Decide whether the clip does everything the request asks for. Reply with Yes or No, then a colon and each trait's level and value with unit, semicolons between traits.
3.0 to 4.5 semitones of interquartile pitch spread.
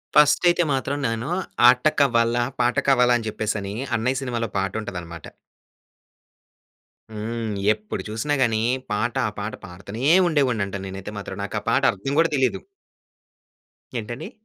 Yes: average, 3.6 semitones